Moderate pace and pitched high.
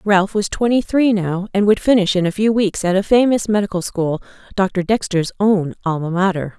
Yes: average, 190 wpm; high, 195 Hz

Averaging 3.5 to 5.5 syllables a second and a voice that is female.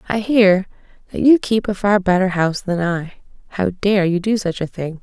Yes: 5.0 syllables/s; female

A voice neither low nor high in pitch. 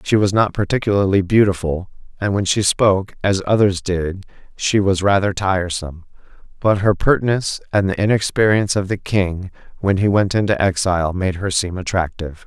No: very low, 95 Hz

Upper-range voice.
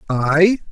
No: medium, 165 Hz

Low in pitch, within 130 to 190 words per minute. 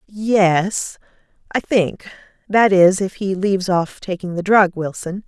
No: high, 190 Hz; slow, 135 wpm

